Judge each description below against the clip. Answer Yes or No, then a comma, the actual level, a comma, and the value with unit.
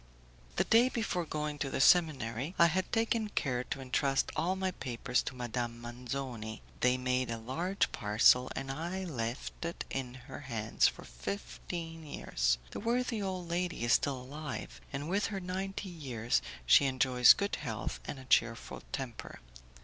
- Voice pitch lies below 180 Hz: Yes, low, 135 Hz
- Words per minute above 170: No, average, 165 wpm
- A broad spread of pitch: Yes, wide, 6.4 semitones